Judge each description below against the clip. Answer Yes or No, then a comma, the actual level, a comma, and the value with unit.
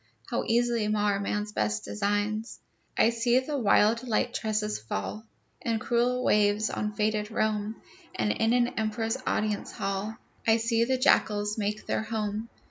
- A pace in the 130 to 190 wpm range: Yes, average, 150 wpm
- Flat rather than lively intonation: Yes, narrow, 1.8 semitones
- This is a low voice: No, high, 215 Hz